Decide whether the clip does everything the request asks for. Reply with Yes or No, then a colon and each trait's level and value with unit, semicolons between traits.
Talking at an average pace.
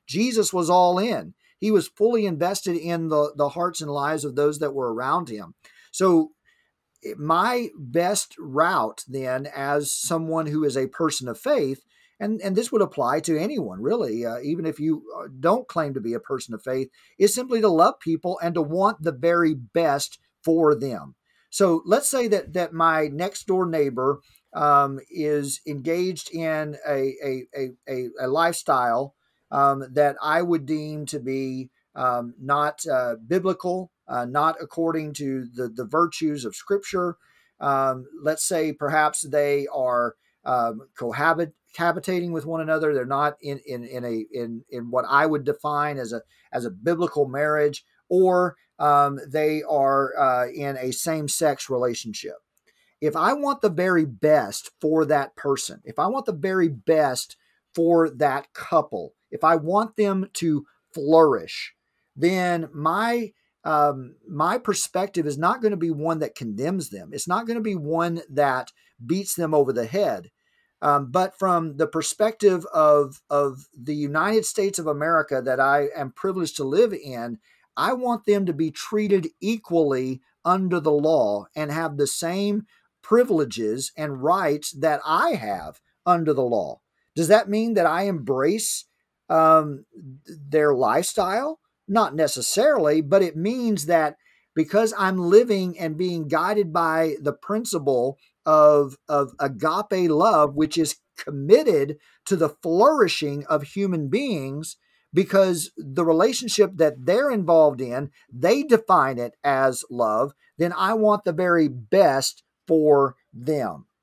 Yes: average, 155 wpm